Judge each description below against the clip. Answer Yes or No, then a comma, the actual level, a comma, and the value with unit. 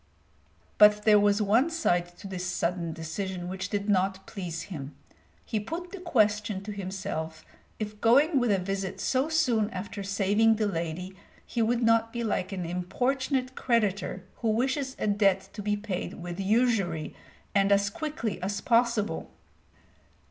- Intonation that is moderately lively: Yes, average, 3.5 semitones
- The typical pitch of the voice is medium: No, high, 205 Hz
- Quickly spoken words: No, average, 155 wpm